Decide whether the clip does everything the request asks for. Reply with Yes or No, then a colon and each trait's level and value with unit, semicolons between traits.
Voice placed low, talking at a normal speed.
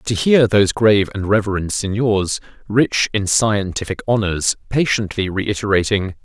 No: low, 105 Hz; slow, 125 wpm